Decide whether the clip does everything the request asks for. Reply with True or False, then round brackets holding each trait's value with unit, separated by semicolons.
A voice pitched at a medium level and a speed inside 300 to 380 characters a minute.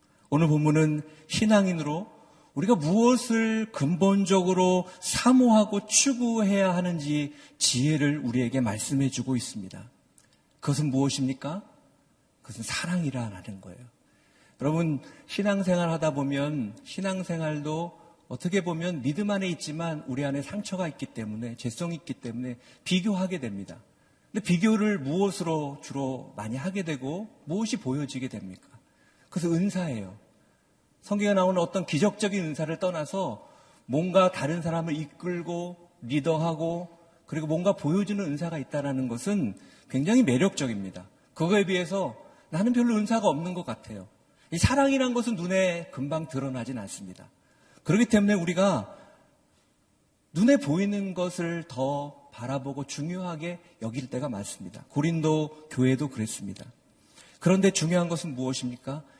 True (165 Hz; 310 characters per minute)